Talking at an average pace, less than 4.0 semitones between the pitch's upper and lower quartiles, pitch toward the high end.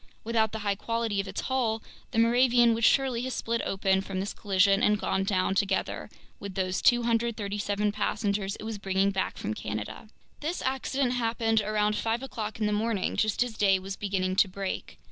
Yes: average, 185 wpm; average, 2.8 semitones; high, 210 Hz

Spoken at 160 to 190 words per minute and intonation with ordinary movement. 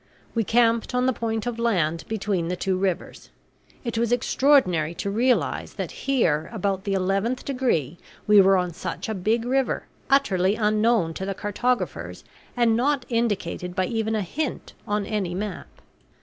Yes: average, 165 wpm; average, 4.1 semitones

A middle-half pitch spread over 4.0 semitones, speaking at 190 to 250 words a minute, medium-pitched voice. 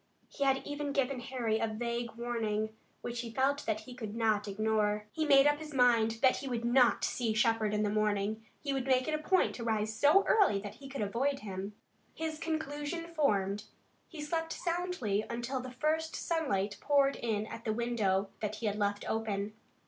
No: average, 4.8 semitones; average, 195 wpm; high, 235 Hz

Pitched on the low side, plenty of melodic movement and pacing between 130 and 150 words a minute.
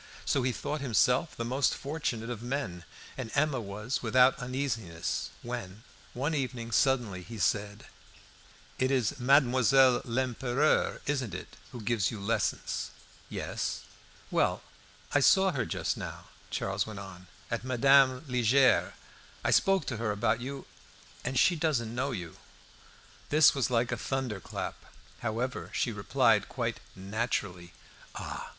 No: low, 120 Hz; average, 3.7 semitones; slow, 135 wpm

